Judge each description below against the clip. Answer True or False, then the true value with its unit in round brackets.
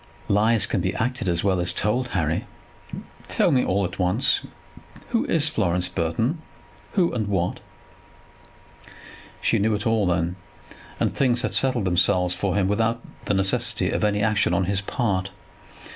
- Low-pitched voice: True (100 Hz)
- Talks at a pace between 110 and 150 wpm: False (160 wpm)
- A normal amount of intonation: True (4.3 semitones)